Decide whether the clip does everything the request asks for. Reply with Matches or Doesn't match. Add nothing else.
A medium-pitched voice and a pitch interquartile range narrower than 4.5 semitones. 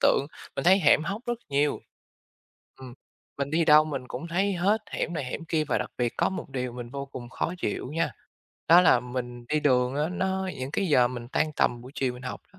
Doesn't match